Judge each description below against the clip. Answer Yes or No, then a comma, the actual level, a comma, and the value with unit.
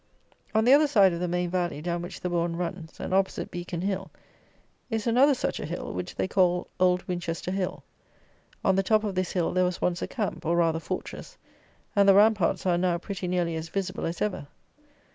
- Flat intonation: Yes, narrow, 2.3 semitones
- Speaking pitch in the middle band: Yes, medium, 180 Hz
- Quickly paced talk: Yes, fast, 210 wpm